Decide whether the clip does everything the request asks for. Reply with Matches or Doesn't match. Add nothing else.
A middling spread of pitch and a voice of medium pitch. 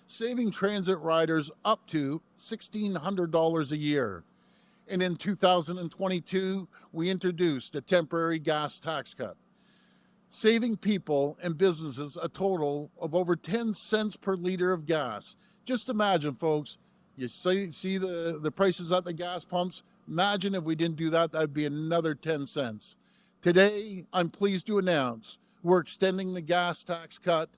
Matches